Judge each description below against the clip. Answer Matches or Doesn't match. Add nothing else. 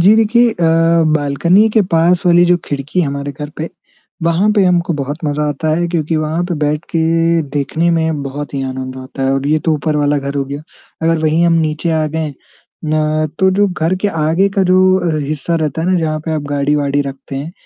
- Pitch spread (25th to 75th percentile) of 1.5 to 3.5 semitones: Matches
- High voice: Doesn't match